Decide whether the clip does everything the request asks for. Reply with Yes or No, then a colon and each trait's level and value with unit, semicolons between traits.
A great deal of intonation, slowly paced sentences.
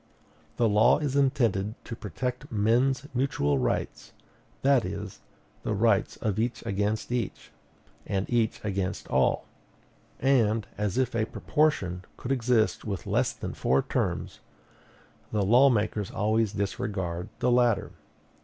No: average, 3.7 semitones; slow, 130 wpm